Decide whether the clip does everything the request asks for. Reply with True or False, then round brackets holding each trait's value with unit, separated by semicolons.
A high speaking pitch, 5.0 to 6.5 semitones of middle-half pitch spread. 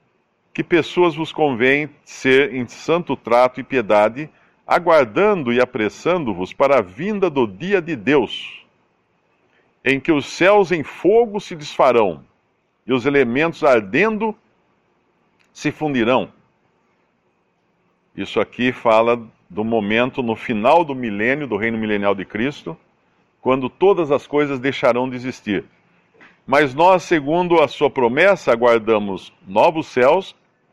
False (135 Hz; 5.5 semitones)